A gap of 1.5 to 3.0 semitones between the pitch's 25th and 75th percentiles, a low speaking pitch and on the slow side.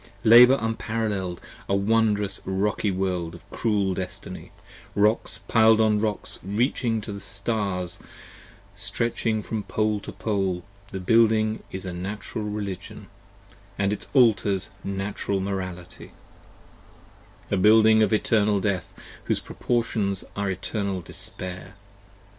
Yes: narrow, 2.4 semitones; low, 100 Hz; slow, 110 wpm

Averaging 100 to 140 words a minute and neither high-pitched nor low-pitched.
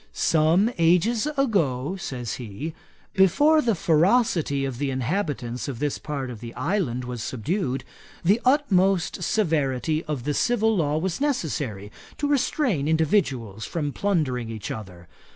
Yes: slow, 135 wpm; medium, 155 Hz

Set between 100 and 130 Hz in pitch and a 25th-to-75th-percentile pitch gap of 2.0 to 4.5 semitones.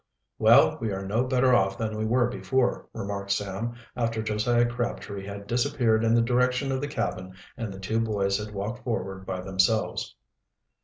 Yes: low, 110 Hz; average, 3.4 semitones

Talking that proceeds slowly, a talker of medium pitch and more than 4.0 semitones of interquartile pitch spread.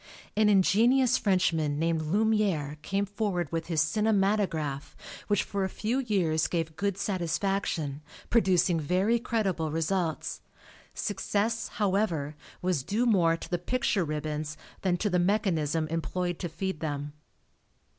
Yes: slow, 130 wpm; medium, 180 Hz; average, 4.4 semitones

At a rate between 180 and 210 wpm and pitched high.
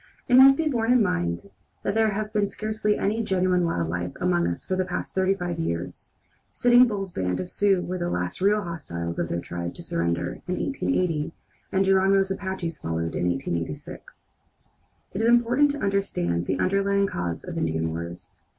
No: average, 185 wpm; medium, 180 Hz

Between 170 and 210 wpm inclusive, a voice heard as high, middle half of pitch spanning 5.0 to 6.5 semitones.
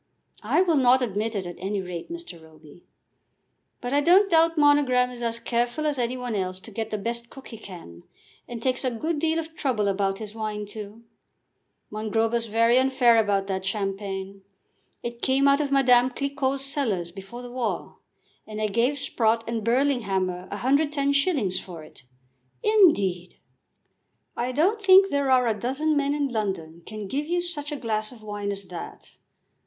Yes: average, 175 wpm; high, 235 Hz; wide, 5.6 semitones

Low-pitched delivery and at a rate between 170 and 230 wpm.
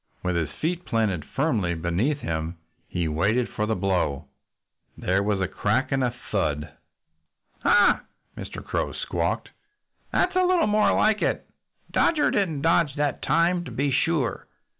No: low, 115 Hz; average, 150 wpm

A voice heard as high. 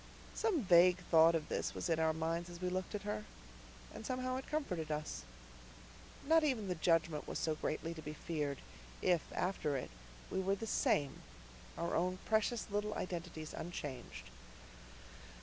No: medium, 175 Hz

